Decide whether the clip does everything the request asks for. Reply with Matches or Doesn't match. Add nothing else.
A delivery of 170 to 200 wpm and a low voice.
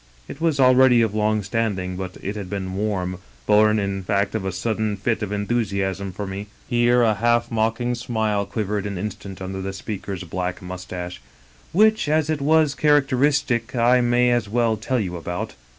Matches